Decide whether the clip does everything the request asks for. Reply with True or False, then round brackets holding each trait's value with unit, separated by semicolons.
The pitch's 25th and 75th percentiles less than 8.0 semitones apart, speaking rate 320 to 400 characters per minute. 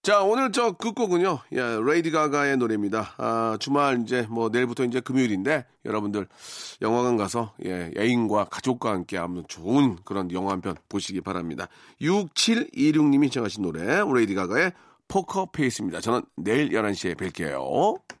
False (8.6 semitones; 335 characters per minute)